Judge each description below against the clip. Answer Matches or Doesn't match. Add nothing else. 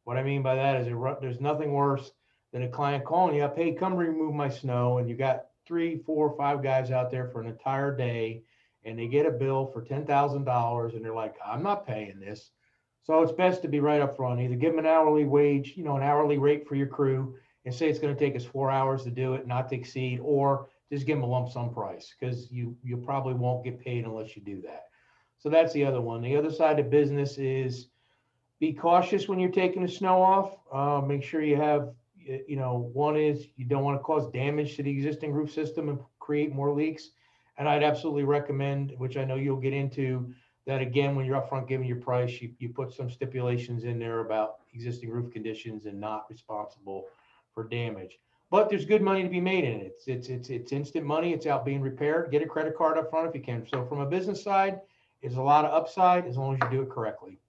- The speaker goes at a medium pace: Doesn't match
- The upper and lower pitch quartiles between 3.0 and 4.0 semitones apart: Matches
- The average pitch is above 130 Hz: Matches